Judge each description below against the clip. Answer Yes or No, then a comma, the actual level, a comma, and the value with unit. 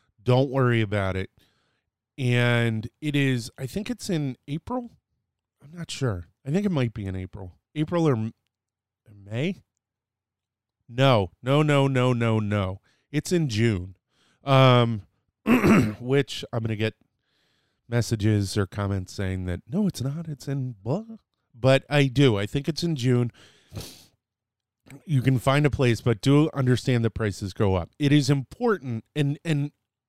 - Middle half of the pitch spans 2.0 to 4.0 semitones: No, average, 4.8 semitones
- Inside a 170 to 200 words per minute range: No, average, 150 wpm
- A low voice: Yes, low, 125 Hz